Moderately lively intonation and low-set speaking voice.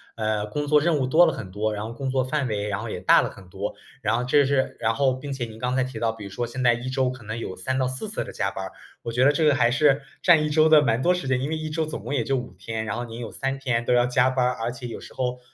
Yes: average, 3.5 semitones; low, 125 Hz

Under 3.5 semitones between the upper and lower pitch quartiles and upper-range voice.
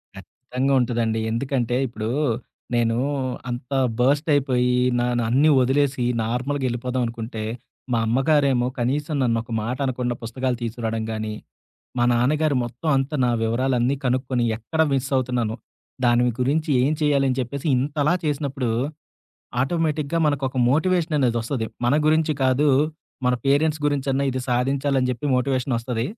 No: average, 2.8 semitones; low, 130 Hz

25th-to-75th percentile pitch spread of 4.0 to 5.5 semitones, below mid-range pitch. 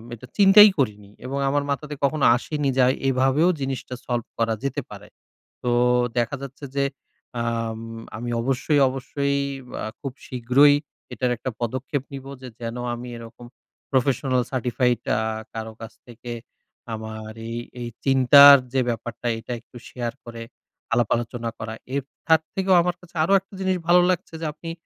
No: average, 3.3 semitones; low, 130 Hz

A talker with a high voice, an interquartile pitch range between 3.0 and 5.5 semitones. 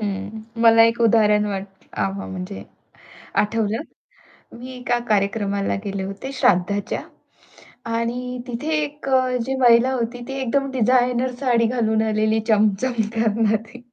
Yes: high, 225 Hz; average, 3.3 semitones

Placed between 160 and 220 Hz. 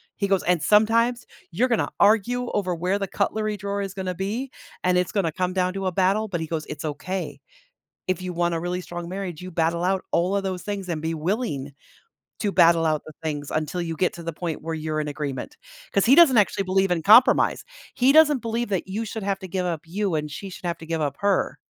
Yes: medium, 185 Hz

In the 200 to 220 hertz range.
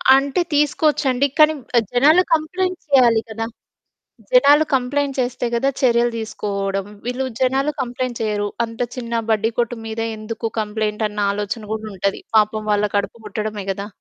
No: high, 235 Hz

